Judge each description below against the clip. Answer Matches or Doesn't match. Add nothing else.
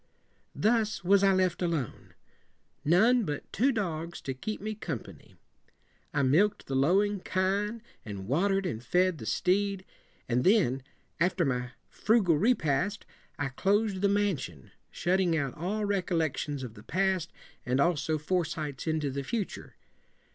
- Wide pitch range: Matches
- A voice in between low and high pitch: Matches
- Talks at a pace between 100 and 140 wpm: Doesn't match